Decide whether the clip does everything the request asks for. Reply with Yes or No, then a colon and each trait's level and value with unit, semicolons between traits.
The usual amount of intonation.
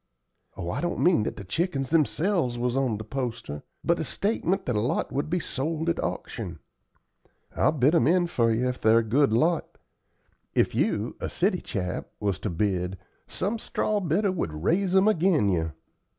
No: wide, 8.3 semitones